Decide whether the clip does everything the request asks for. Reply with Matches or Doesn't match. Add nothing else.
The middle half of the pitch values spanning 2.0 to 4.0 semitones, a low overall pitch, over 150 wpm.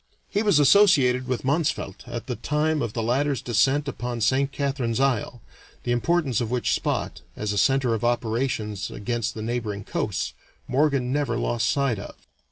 Matches